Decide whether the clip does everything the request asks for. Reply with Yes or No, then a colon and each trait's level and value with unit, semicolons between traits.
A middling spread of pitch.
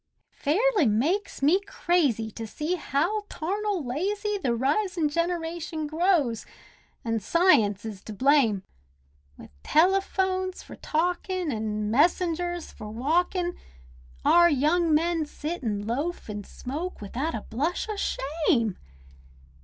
No: wide, 7.0 semitones